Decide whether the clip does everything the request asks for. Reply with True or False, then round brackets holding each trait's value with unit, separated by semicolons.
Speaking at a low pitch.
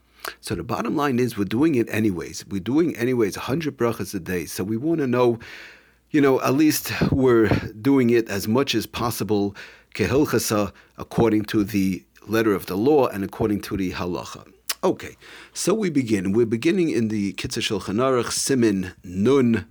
True (110 Hz)